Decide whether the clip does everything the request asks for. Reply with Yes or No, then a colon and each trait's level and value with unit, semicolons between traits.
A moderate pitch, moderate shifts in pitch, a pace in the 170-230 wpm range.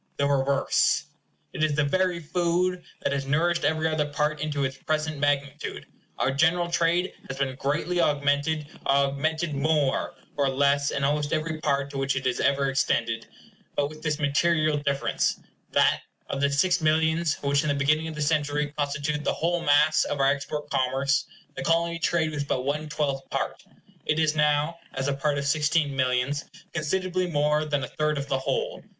No: medium, 150 Hz; narrow, 2.0 semitones; average, 180 wpm